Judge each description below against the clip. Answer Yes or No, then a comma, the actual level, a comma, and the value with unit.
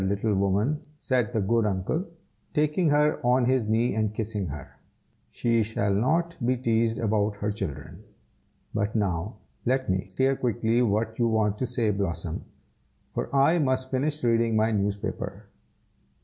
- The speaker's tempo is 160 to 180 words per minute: No, average, 150 wpm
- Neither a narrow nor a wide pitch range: Yes, average, 4.0 semitones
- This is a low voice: Yes, low, 115 Hz